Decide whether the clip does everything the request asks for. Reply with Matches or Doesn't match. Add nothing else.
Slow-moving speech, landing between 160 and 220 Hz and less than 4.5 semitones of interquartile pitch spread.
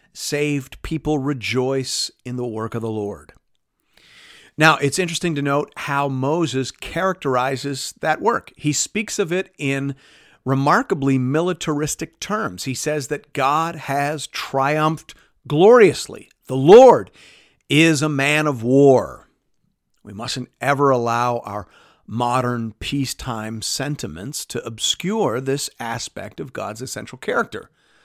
Doesn't match